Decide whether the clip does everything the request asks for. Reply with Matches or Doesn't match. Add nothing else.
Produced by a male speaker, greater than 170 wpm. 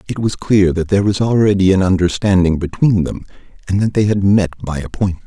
Matches